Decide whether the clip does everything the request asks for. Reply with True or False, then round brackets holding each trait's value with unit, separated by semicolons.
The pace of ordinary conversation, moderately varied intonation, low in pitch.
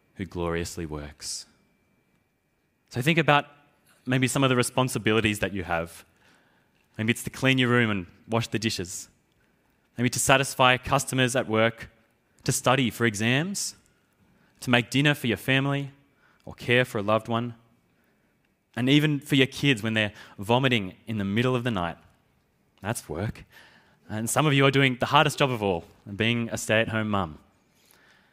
True (165 wpm; 4.1 semitones; 120 Hz)